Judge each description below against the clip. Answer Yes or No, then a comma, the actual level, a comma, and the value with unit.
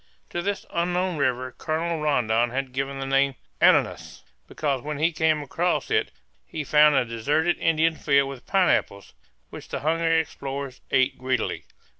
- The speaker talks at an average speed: Yes, average, 155 wpm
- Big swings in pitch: No, average, 3.5 semitones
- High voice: No, medium, 145 Hz